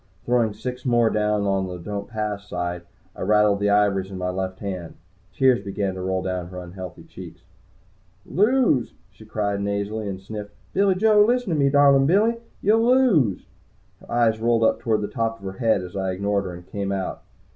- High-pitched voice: No, low, 105 Hz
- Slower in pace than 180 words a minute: No, average, 195 wpm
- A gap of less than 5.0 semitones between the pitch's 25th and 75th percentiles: Yes, average, 4.6 semitones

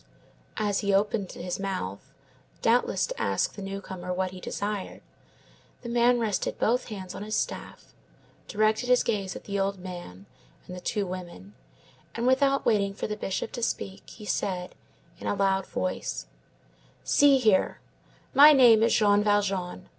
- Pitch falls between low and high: No, high, 200 Hz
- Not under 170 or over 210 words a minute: No, average, 160 wpm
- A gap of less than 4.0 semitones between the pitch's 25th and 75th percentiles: Yes, average, 3.3 semitones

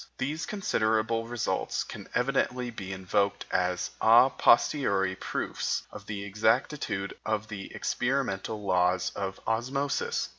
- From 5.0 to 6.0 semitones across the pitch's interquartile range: No, average, 4.2 semitones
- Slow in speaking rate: Yes, slow, 115 wpm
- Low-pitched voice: Yes, low, 110 Hz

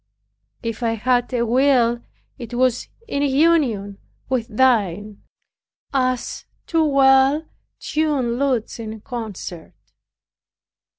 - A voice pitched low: No, high, 245 Hz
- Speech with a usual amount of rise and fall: Yes, average, 3.1 semitones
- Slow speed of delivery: Yes, slow, 100 wpm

